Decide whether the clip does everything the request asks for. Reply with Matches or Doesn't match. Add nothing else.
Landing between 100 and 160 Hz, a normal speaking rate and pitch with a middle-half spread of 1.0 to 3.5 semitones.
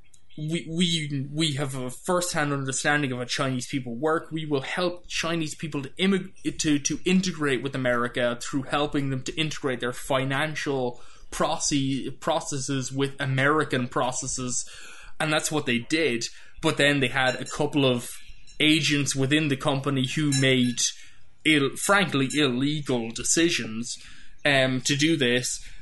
Matches